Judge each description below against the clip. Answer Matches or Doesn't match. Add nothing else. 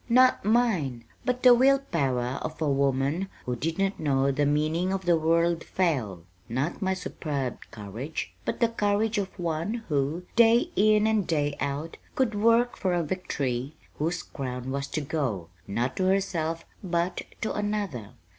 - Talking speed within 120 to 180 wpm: Matches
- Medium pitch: Matches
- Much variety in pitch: Matches